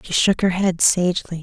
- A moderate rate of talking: No, fast, 210 wpm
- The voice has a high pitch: No, medium, 180 Hz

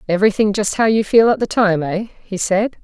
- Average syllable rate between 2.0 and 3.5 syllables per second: No, 5.5 syllables/s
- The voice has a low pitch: No, high, 205 Hz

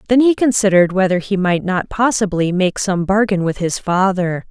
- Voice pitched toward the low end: No, high, 195 Hz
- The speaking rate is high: No, average, 185 wpm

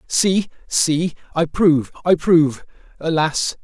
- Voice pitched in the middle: Yes, medium, 160 Hz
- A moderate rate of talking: No, slow, 115 wpm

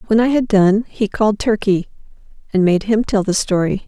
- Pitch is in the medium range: No, high, 205 Hz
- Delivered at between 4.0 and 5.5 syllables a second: Yes, 5.3 syllables/s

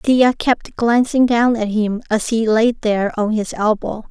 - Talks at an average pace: Yes, average, 190 wpm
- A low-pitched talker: No, high, 225 Hz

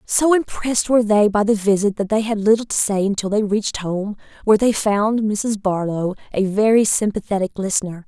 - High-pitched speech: Yes, high, 210 Hz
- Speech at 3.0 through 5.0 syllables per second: No, 5.5 syllables/s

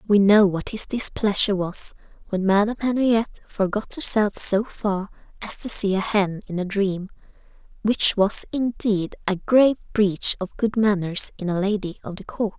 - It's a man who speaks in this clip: No, female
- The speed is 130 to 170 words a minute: Yes, average, 165 wpm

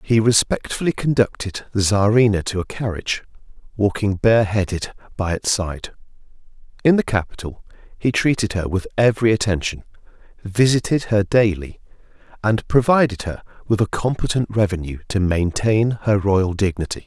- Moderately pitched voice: No, low, 105 Hz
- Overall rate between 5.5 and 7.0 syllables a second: No, 5.1 syllables/s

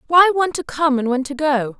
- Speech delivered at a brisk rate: Yes, fast, 265 wpm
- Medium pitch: No, very high, 285 Hz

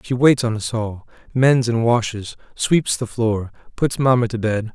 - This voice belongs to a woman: No, male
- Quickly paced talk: No, average, 190 wpm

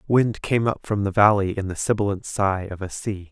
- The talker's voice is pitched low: Yes, low, 100 Hz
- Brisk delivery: Yes, fast, 235 wpm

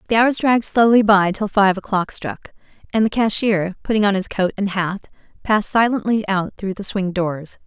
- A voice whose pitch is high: Yes, high, 200 Hz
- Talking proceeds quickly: No, average, 195 wpm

